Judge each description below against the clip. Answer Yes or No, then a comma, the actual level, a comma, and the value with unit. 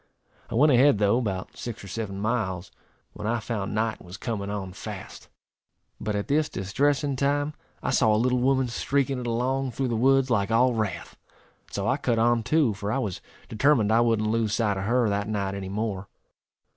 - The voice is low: Yes, low, 115 Hz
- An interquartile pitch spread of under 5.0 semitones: Yes, average, 3.8 semitones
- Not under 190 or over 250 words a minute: Yes, average, 200 wpm